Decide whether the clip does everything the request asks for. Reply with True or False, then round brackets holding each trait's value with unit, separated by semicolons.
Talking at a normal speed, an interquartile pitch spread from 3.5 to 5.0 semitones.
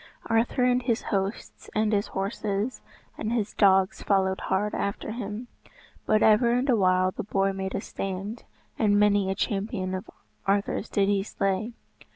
False (160 wpm; 2.4 semitones)